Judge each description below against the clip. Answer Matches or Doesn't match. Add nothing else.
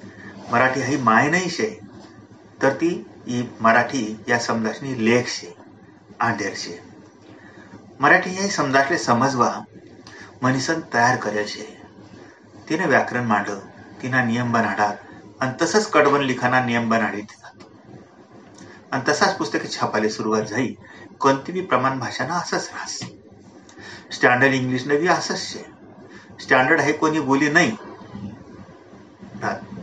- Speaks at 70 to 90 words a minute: Doesn't match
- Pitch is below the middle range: Matches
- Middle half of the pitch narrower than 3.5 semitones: Doesn't match